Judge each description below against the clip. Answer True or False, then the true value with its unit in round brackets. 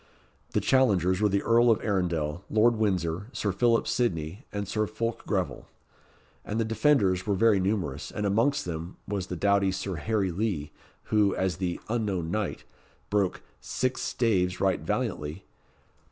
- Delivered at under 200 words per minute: True (155 wpm)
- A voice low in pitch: True (100 Hz)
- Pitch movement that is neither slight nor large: True (3.4 semitones)